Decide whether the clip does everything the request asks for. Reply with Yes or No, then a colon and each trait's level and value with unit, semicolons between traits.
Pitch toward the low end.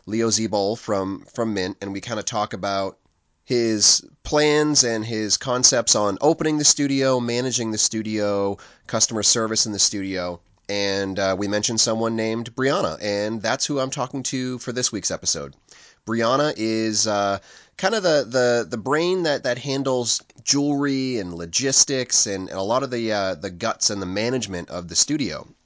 Yes: low, 115 Hz